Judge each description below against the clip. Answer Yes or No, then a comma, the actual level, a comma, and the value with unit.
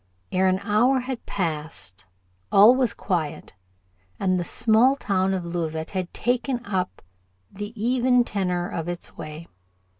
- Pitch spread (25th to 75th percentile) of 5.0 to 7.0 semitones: Yes, wide, 5.6 semitones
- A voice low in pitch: No, high, 190 Hz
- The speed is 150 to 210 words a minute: No, average, 140 wpm